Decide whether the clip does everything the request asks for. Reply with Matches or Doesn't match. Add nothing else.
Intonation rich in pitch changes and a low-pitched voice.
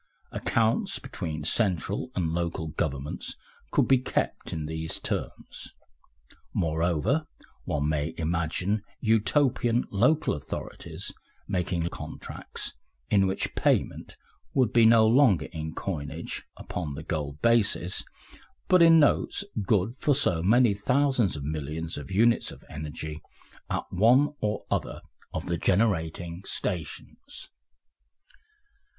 Matches